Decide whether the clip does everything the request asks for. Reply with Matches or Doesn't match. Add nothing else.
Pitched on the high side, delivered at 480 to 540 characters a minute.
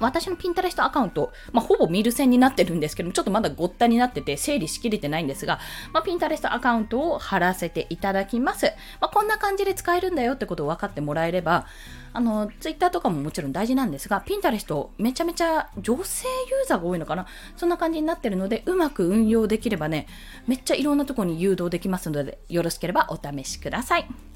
Matches